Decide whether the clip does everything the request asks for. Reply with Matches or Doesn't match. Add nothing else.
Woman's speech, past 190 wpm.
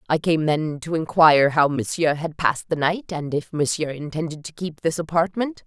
Matches